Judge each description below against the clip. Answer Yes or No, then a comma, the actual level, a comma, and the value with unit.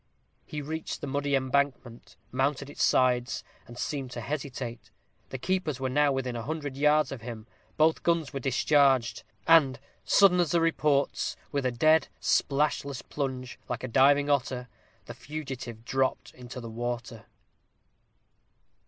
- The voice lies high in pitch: No, low, 135 Hz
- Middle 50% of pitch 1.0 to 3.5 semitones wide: Yes, average, 3.0 semitones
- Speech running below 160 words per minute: Yes, average, 145 wpm